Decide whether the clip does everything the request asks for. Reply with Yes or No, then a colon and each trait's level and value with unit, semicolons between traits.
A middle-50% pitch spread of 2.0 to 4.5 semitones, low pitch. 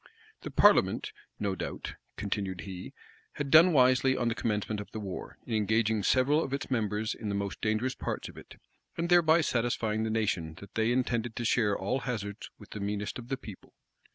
Yes: average, 3.8 semitones; low, 110 Hz